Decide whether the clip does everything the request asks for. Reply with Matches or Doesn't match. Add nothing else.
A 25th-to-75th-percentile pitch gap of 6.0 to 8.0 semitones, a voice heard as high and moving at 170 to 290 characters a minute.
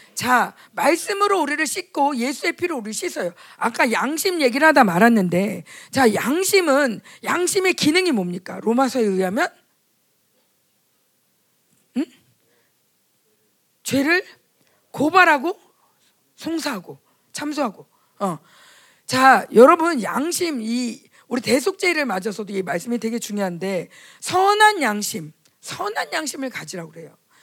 Matches